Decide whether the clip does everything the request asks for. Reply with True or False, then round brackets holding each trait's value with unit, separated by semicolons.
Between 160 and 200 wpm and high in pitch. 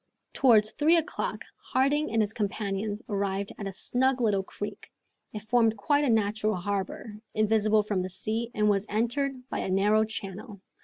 True (165 wpm; 215 Hz)